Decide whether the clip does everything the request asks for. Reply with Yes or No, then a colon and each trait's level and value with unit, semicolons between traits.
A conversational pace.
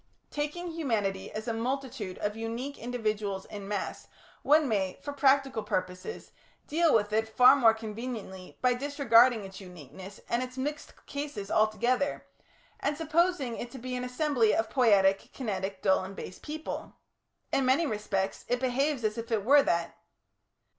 Yes: average, 155 wpm